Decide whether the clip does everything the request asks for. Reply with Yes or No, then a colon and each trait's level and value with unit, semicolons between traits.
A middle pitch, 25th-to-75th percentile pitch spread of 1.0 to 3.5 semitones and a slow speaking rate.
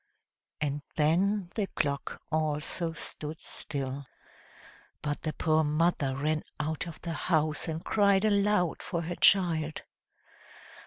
Yes: medium, 160 Hz; average, 3.0 semitones; slow, 120 wpm